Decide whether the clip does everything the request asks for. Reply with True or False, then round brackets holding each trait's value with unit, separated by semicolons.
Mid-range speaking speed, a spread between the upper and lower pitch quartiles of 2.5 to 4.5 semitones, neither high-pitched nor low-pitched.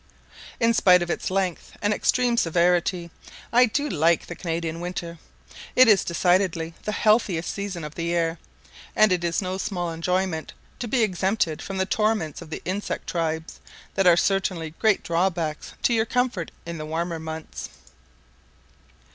True (160 wpm; 3.4 semitones; 180 Hz)